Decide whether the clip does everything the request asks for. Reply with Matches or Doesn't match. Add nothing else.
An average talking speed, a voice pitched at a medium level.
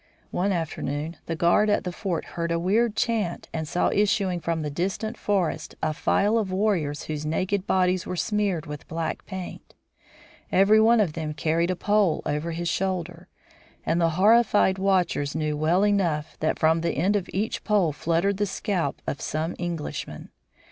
Matches